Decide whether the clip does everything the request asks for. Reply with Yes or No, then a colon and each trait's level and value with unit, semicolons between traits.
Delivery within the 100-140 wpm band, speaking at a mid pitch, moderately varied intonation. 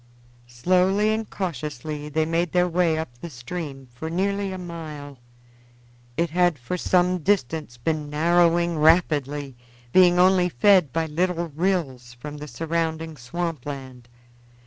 Yes: slow, 135 wpm; medium, 165 Hz; average, 3.5 semitones